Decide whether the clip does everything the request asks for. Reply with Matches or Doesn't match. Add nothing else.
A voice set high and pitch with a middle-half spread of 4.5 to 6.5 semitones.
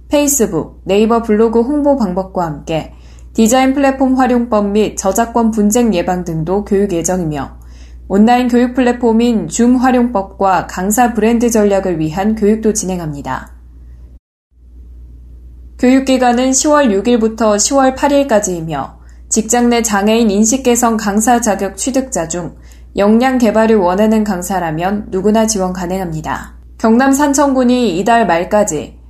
Matches